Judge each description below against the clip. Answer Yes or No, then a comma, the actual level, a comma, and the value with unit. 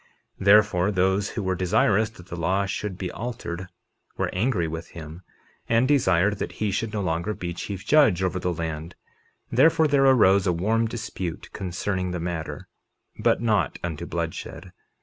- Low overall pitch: Yes, very low, 95 Hz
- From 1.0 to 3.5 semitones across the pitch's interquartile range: No, average, 3.9 semitones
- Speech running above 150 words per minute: Yes, average, 170 wpm